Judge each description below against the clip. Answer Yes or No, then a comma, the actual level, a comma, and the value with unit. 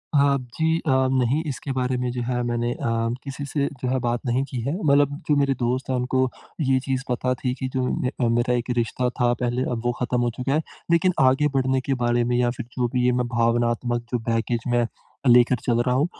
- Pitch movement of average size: No, narrow, 1.7 semitones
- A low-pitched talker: Yes, low, 125 Hz